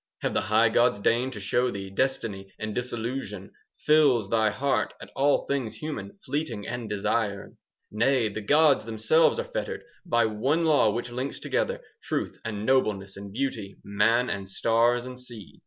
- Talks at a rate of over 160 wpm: Yes, average, 170 wpm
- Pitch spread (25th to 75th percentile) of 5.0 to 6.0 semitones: No, average, 4.3 semitones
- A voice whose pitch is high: No, low, 115 Hz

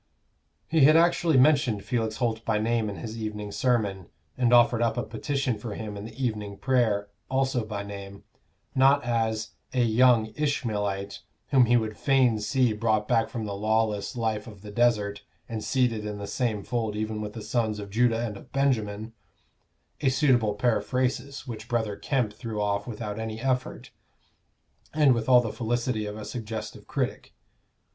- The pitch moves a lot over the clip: No, average, 2.8 semitones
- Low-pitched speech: Yes, low, 115 Hz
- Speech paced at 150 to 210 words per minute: Yes, average, 170 wpm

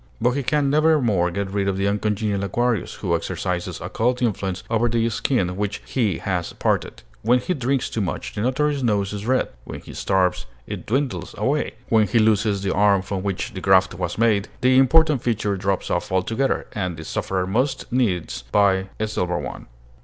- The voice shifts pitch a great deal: No, average, 4.4 semitones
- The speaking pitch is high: No, low, 105 Hz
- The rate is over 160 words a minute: Yes, average, 190 wpm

